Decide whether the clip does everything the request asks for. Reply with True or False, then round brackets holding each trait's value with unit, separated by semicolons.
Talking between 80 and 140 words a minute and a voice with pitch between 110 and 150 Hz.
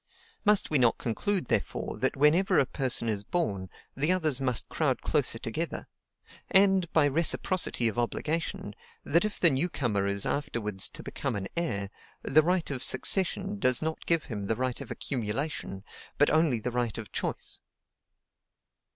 False (160 wpm; 135 Hz)